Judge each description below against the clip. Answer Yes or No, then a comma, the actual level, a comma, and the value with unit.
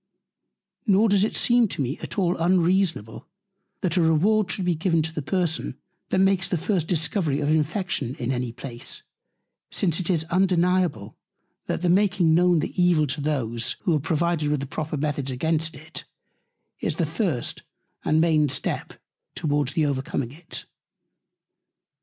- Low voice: No, medium, 160 Hz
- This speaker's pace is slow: No, average, 160 wpm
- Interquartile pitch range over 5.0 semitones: No, average, 3.8 semitones